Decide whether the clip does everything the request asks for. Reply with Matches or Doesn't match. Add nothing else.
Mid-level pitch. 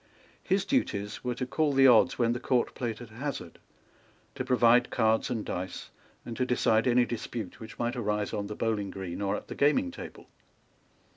Doesn't match